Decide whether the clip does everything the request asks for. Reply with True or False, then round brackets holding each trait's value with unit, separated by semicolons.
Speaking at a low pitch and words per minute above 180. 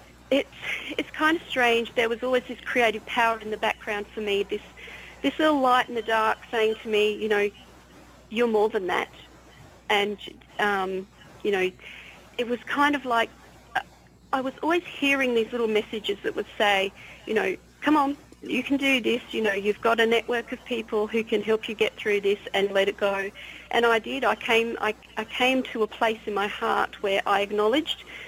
False (230 Hz; 200 wpm)